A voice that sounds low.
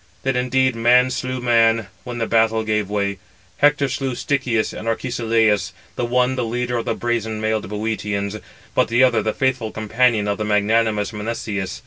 Yes: low, 115 Hz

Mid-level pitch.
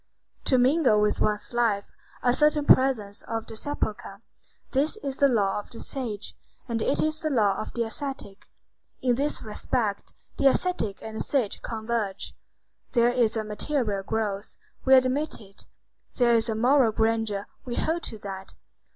No: high, 230 Hz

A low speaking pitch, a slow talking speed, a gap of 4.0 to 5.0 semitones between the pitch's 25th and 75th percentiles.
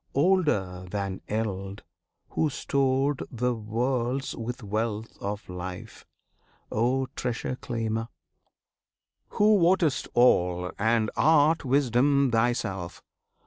Yes: low, 120 Hz; slow, 95 wpm; average, 4.7 semitones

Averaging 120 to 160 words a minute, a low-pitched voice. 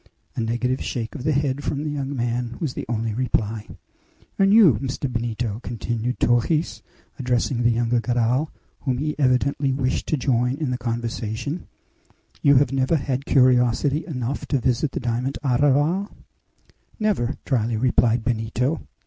Yes: average, 150 wpm; low, 125 Hz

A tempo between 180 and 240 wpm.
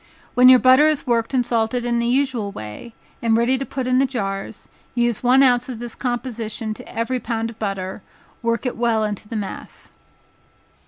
Yes: average, 195 wpm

